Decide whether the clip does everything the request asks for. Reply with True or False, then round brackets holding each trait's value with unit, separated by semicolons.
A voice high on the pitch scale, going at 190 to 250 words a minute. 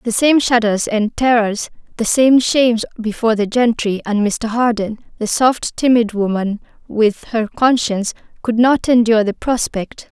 False (230 Hz; 145 wpm)